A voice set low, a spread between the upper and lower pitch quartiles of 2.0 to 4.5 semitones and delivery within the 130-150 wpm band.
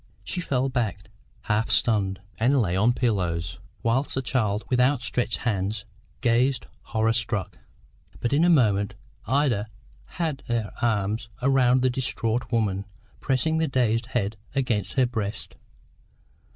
Yes: low, 115 Hz; average, 3.6 semitones; average, 140 wpm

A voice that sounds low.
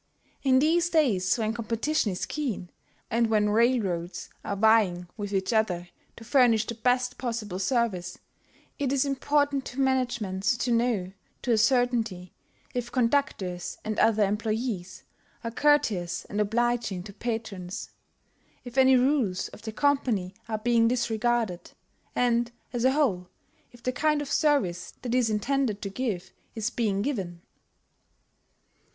No: high, 230 Hz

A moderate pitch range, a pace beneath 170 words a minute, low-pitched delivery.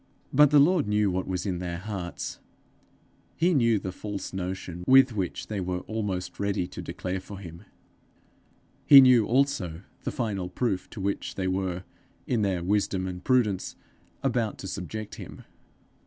Yes: average, 4.1 semitones; average, 160 wpm; low, 100 Hz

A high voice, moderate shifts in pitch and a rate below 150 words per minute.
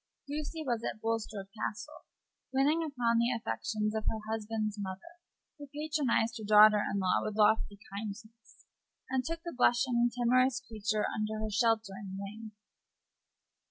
Yes: high, 225 Hz; average, 3.0 semitones; average, 140 wpm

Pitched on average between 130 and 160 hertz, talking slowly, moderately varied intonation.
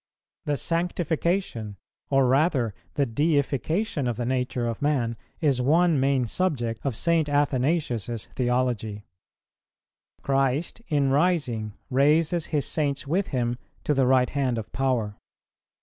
Yes: low, 135 Hz; slow, 125 wpm; average, 3.9 semitones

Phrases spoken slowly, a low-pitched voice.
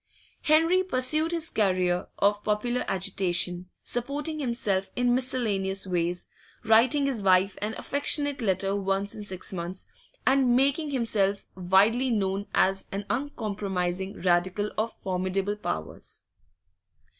No: slow, 120 wpm; high, 205 Hz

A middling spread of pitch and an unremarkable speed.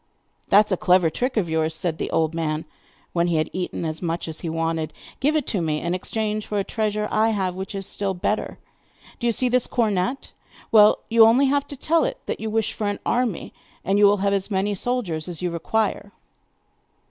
No: average, 4.6 semitones; fast, 220 wpm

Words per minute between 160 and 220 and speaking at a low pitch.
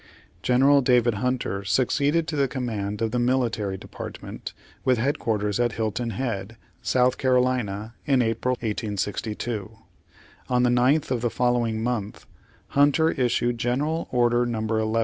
No: average, 145 wpm; low, 120 Hz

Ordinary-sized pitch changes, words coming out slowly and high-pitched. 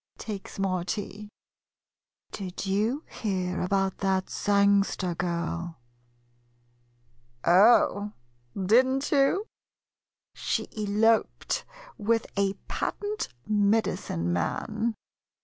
Yes: average, 3.0 semitones; slow, 80 wpm; high, 200 Hz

